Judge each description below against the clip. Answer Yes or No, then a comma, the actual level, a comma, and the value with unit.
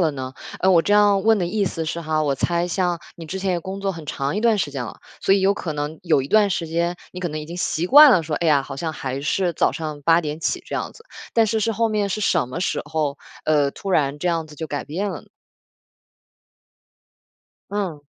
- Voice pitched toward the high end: No, medium, 170 Hz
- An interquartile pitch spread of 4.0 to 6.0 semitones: Yes, average, 4.4 semitones